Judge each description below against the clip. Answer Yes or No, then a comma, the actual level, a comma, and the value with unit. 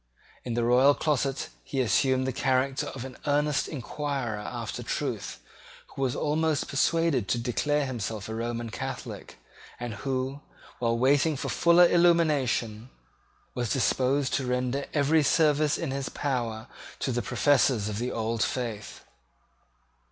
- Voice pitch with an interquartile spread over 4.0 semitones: No, average, 3.3 semitones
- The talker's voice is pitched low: Yes, low, 130 Hz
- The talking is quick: No, average, 140 wpm